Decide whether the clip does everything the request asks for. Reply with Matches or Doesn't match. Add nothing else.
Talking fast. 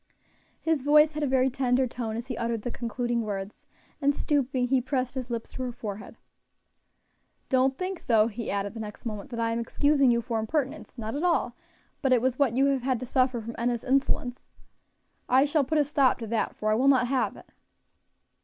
Matches